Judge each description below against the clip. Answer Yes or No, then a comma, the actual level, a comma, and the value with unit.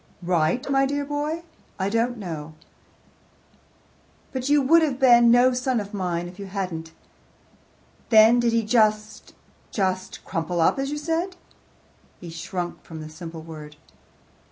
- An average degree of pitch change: No, wide, 7.0 semitones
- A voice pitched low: No, high, 215 Hz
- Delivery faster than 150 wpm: No, average, 145 wpm